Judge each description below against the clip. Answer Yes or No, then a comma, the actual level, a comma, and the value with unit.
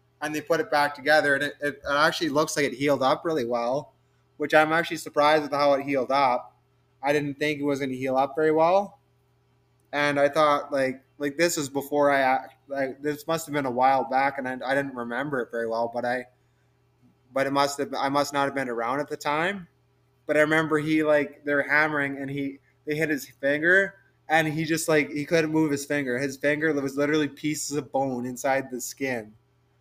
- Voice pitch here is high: No, medium, 140 Hz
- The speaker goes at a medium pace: No, fast, 220 wpm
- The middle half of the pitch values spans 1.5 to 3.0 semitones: Yes, narrow, 2.5 semitones